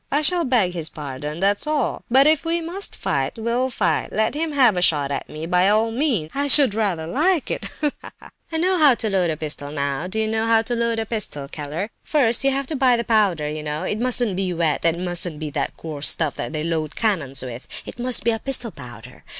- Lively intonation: Yes, wide, 8.4 semitones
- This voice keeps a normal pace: No, fast, 240 wpm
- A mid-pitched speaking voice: No, high, 210 Hz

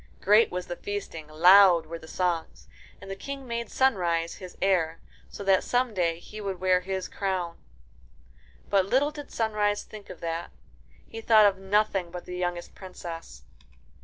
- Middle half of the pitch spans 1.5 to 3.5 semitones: Yes, average, 3.2 semitones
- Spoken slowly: No, average, 165 wpm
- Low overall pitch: No, high, 190 Hz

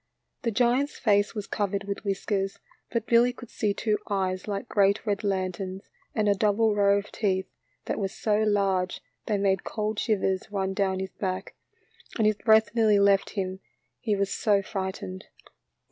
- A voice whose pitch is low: No, high, 200 Hz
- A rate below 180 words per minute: Yes, average, 170 wpm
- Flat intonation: Yes, narrow, 1.8 semitones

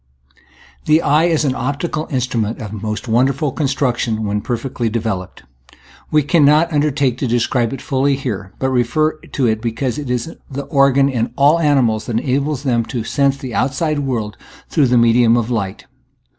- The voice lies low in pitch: Yes, low, 130 Hz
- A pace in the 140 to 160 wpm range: No, average, 170 wpm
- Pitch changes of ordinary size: Yes, average, 3.5 semitones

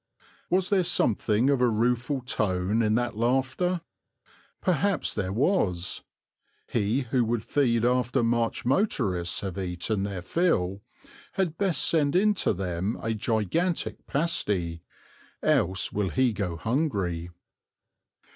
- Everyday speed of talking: No, slow, 125 wpm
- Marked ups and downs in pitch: Yes, wide, 6.5 semitones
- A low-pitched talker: Yes, low, 115 Hz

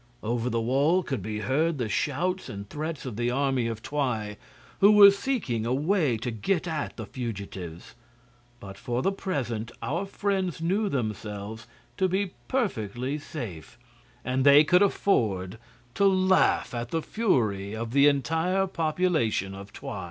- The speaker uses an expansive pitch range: Yes, wide, 8.2 semitones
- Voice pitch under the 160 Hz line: Yes, low, 135 Hz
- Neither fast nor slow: Yes, average, 155 wpm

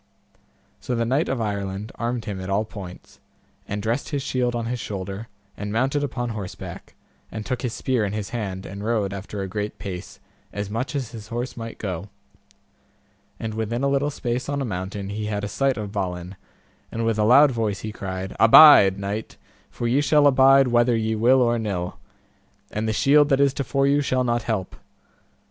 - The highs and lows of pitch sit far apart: No, average, 3.9 semitones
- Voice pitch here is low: Yes, low, 115 Hz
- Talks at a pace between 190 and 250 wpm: Yes, average, 200 wpm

